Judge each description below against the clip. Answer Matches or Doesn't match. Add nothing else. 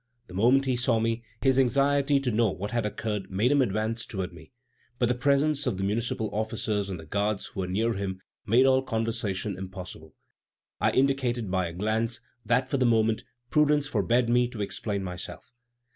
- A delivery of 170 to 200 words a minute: Matches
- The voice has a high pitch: Doesn't match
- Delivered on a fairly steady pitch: Doesn't match